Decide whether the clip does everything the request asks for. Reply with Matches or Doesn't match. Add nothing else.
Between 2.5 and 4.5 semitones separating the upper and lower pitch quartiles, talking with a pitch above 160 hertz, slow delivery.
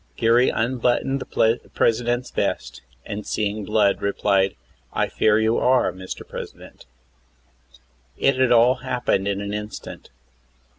Doesn't match